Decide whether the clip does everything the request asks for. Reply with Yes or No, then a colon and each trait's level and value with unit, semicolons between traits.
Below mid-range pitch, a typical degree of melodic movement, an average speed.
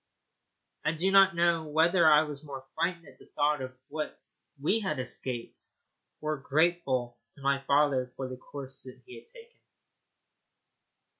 No: medium, 150 Hz; average, 4.0 semitones; average, 150 wpm